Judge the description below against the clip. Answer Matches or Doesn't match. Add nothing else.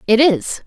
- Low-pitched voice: Doesn't match